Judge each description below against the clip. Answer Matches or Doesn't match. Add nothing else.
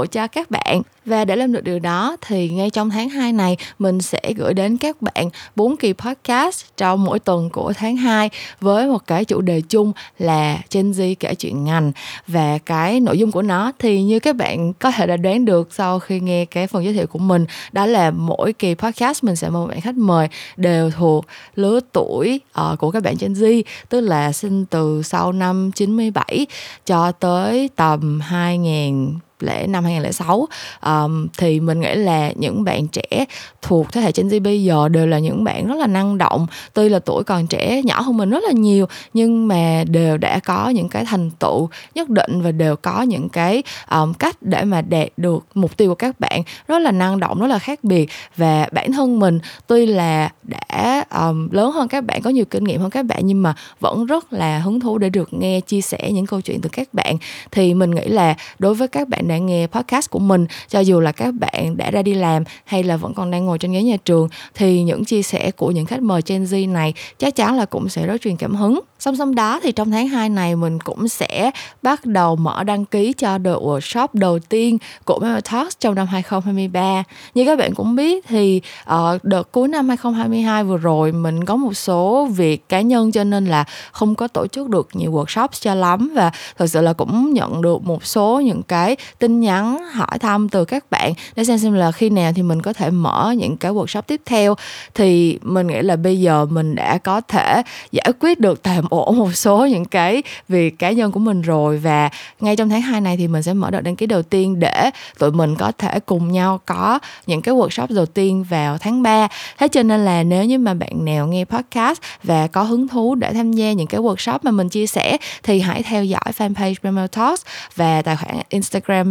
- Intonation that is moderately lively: Matches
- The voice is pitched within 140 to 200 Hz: Matches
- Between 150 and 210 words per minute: Doesn't match